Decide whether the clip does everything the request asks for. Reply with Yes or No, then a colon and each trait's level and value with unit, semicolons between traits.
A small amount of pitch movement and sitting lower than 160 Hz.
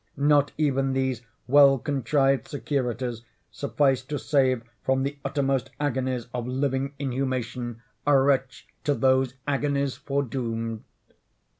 Yes: narrow, 1.7 semitones; low, 135 Hz